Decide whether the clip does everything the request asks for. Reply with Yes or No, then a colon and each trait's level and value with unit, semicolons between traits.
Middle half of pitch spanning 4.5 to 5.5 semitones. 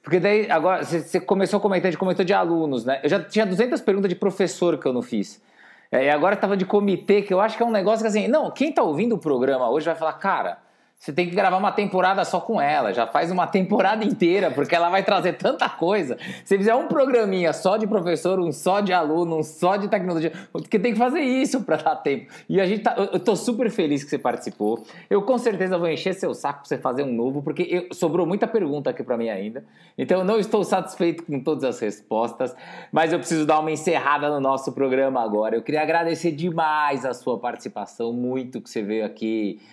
Yes: average, 5.0 semitones